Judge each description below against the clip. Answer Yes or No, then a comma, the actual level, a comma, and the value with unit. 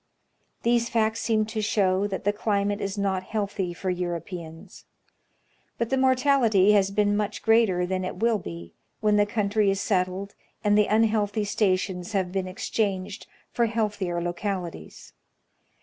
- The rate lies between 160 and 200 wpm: No, average, 150 wpm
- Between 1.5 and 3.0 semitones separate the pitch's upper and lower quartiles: Yes, average, 2.7 semitones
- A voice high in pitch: Yes, high, 205 Hz